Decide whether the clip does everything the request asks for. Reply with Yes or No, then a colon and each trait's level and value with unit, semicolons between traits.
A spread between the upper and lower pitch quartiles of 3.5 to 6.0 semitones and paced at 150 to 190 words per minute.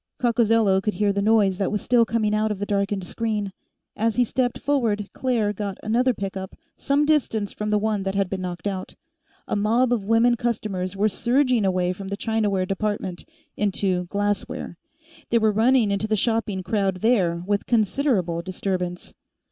No: average, 2.9 semitones; average, 175 wpm